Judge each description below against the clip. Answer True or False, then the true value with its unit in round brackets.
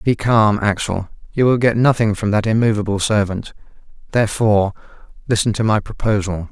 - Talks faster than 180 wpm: False (145 wpm)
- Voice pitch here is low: True (105 Hz)